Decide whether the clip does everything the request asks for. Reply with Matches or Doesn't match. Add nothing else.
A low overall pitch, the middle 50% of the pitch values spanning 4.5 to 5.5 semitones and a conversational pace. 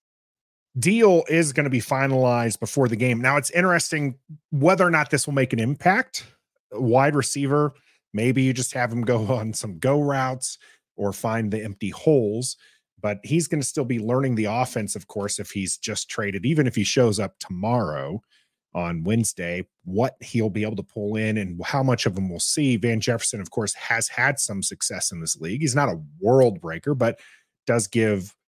Matches